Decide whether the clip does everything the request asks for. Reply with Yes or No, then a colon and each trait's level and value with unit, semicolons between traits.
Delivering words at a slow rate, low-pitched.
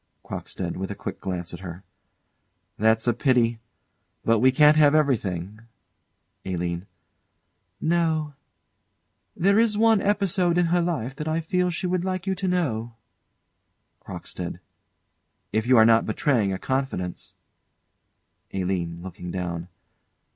Yes: slow, 130 wpm; low, 125 Hz